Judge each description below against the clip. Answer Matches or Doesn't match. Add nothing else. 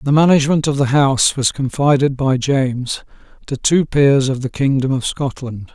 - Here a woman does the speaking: Doesn't match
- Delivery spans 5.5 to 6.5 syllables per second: Doesn't match